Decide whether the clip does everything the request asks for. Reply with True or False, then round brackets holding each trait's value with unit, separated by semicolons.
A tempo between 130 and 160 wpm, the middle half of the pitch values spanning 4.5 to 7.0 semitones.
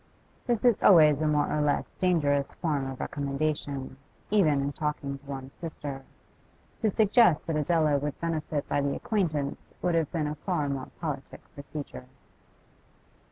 False (155 wpm; 2.8 semitones)